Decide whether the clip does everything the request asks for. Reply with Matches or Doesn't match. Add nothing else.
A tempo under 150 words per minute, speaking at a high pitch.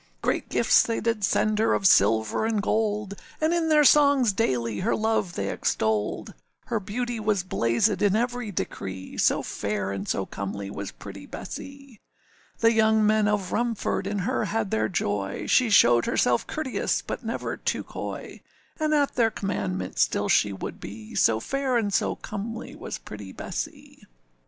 Doesn't match